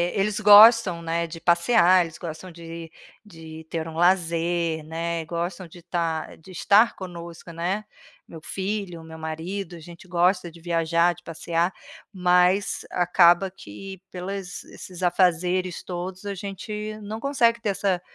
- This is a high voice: No, medium, 175 Hz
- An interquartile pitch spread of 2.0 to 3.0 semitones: Yes, narrow, 2.5 semitones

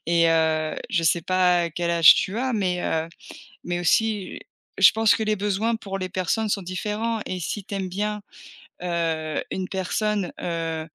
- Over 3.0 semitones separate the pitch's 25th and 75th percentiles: Yes, average, 3.7 semitones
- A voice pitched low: No, medium, 185 Hz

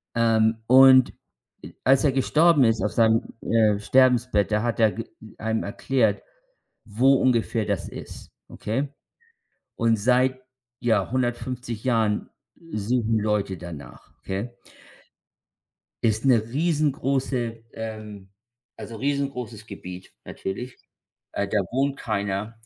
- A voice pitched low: Yes, low, 115 Hz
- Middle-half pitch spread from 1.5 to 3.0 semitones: No, average, 3.4 semitones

